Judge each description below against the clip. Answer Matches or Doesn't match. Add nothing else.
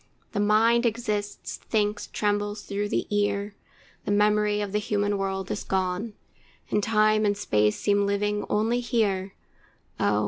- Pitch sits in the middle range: Doesn't match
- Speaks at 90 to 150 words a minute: Matches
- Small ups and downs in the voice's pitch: Matches